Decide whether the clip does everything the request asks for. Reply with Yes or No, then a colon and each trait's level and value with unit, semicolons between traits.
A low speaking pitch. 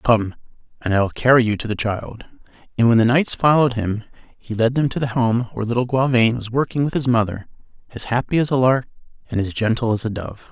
Yes: low, 120 Hz